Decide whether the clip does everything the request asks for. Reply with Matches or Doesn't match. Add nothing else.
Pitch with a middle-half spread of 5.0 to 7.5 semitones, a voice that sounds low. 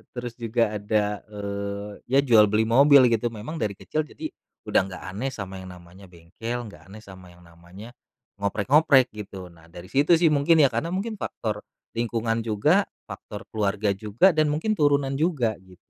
Matches